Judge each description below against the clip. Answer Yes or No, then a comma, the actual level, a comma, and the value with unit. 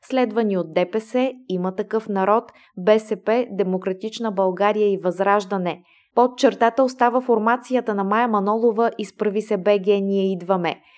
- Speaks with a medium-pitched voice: No, high, 210 Hz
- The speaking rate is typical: Yes, average, 125 wpm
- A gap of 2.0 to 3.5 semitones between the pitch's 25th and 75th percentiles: Yes, average, 3.0 semitones